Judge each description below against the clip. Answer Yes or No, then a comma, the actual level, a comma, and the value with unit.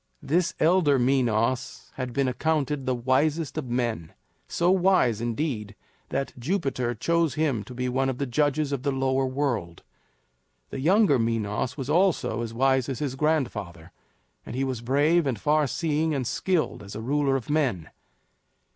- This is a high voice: No, low, 135 Hz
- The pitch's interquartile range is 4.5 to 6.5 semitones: No, average, 4.1 semitones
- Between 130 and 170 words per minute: Yes, average, 165 wpm